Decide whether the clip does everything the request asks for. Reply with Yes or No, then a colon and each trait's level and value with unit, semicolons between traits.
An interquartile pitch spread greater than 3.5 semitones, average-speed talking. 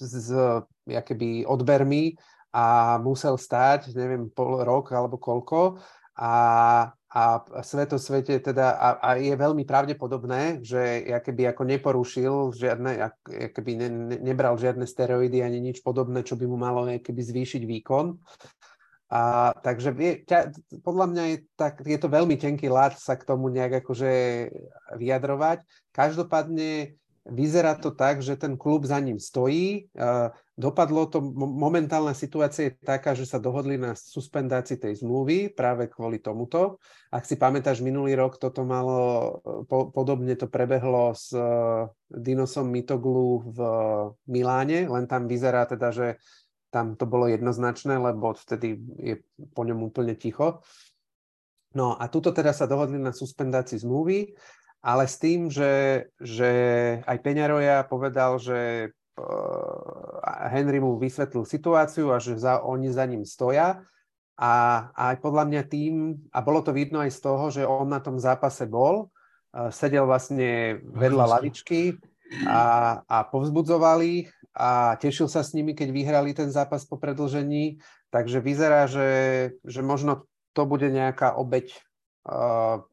No: average, 2.9 semitones; average, 140 wpm